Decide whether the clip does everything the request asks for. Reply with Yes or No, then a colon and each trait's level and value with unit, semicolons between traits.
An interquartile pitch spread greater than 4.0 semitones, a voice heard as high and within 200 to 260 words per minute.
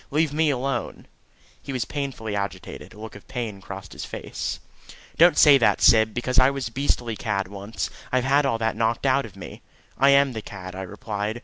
No: average, 4.9 semitones; low, 115 Hz; fast, 205 wpm